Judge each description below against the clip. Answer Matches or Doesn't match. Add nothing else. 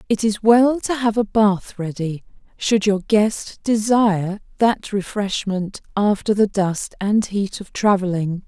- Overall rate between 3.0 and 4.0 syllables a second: Matches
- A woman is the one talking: Matches